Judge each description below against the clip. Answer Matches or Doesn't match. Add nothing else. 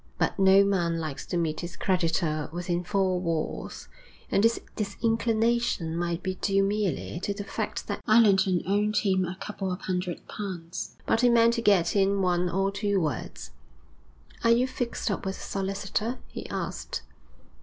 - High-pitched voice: Matches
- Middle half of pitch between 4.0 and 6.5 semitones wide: Doesn't match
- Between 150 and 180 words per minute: Matches